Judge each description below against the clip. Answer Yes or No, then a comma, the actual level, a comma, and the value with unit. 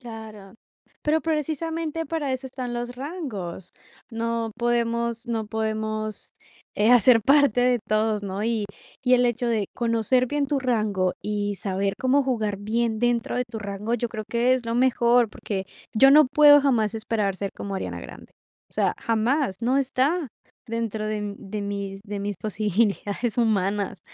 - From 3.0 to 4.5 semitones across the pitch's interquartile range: Yes, average, 3.3 semitones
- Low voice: No, high, 230 Hz